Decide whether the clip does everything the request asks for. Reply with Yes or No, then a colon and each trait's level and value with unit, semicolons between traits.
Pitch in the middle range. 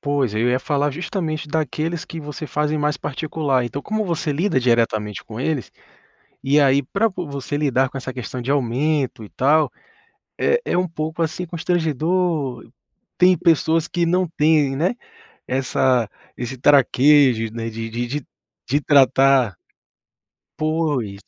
Yes: medium, 145 Hz